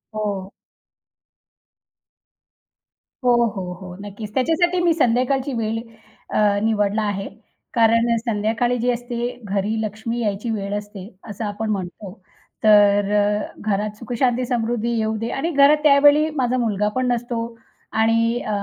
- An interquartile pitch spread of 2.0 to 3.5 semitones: Yes, average, 3.0 semitones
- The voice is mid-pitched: No, high, 225 Hz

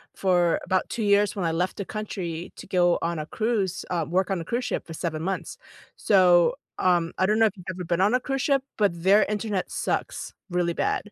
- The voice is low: No, medium, 185 Hz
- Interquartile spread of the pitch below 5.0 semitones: Yes, average, 3.2 semitones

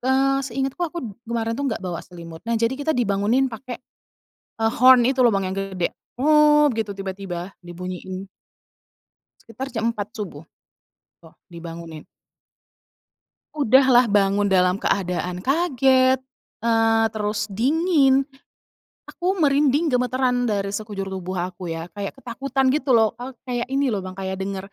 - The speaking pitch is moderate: No, high, 225 Hz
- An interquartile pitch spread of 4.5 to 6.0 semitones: Yes, wide, 5.5 semitones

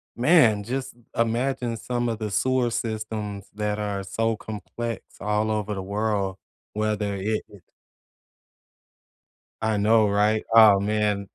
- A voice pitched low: Yes, low, 110 Hz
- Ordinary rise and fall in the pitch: No, narrow, 1.9 semitones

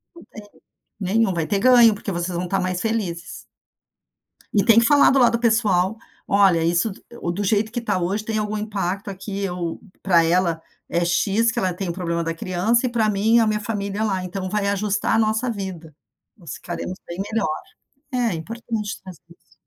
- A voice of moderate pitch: No, high, 200 Hz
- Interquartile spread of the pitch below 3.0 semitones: No, average, 3.8 semitones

